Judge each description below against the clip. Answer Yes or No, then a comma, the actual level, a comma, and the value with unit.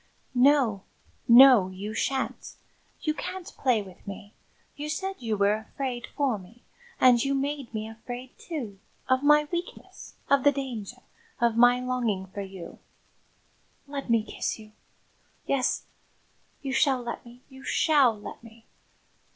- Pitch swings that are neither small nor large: Yes, average, 4.2 semitones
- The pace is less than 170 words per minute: Yes, average, 145 wpm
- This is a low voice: No, high, 245 Hz